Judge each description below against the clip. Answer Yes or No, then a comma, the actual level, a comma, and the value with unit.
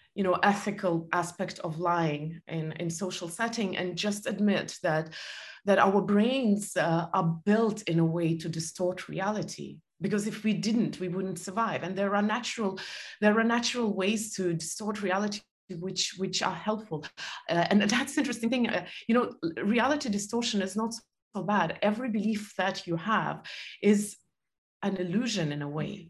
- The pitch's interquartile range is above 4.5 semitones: No, average, 3.5 semitones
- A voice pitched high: Yes, high, 200 Hz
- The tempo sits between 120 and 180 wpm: Yes, average, 170 wpm